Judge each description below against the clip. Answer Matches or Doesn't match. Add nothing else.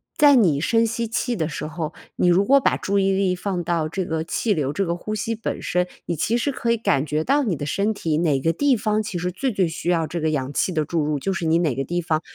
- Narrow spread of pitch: Doesn't match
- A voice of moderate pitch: Matches